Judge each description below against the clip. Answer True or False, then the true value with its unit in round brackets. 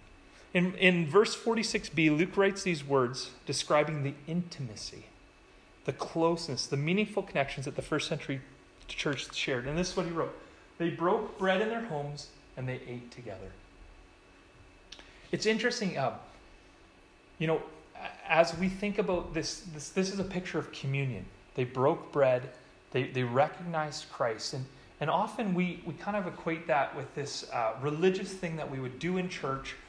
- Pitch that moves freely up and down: True (5.7 semitones)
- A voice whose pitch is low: False (155 Hz)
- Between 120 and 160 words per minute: False (170 wpm)